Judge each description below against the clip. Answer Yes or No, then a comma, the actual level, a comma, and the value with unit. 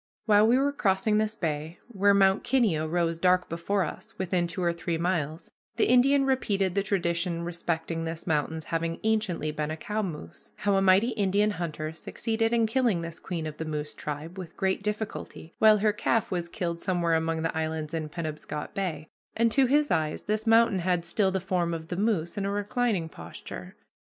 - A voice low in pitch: No, medium, 180 Hz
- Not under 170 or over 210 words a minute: Yes, average, 195 wpm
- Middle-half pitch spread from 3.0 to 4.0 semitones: No, average, 4.4 semitones